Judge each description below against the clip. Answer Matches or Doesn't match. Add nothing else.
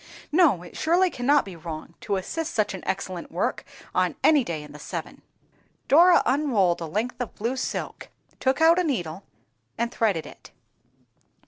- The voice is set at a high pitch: Matches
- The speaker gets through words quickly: Doesn't match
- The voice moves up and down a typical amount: Doesn't match